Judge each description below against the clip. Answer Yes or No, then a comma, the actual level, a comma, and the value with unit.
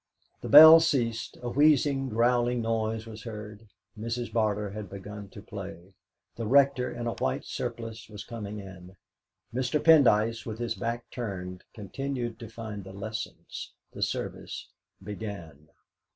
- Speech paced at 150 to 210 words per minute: No, average, 140 wpm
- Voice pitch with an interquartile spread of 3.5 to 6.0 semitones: No, average, 2.8 semitones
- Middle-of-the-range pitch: No, low, 115 Hz